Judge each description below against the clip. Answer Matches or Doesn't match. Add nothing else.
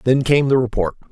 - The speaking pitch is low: Matches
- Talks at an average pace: Doesn't match